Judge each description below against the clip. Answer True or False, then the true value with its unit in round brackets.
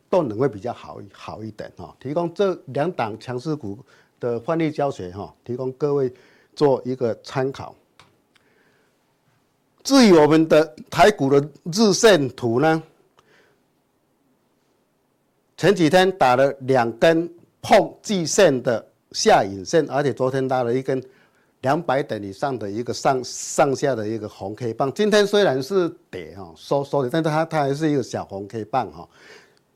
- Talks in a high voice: False (140 Hz)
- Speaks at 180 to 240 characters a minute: True (220 characters per minute)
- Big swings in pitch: False (4.9 semitones)